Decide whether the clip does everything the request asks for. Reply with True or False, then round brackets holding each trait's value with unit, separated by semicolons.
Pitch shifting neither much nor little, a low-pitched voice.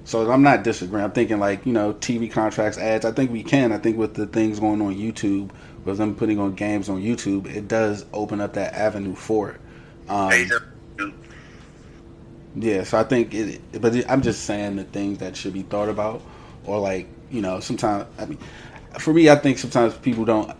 False (2.3 semitones; 105 Hz)